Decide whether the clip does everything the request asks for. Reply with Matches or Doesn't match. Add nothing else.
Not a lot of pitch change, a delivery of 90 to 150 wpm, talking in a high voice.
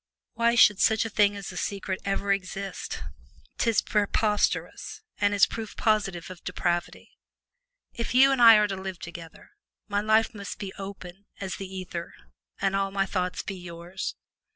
Doesn't match